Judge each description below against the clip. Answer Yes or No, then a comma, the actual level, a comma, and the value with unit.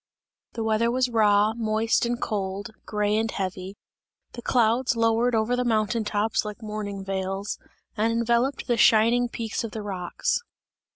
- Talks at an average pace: Yes, average, 155 wpm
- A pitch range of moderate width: No, narrow, 2.2 semitones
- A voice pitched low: No, high, 220 Hz